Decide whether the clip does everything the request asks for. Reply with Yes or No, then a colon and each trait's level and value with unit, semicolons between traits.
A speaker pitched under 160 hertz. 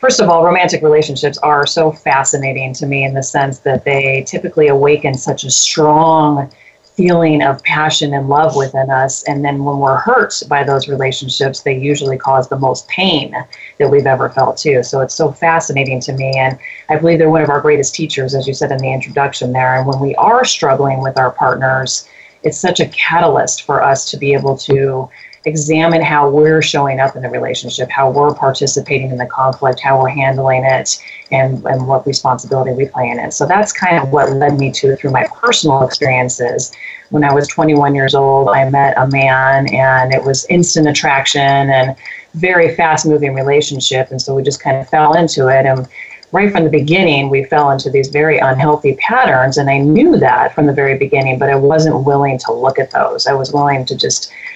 Yes: medium, 140 Hz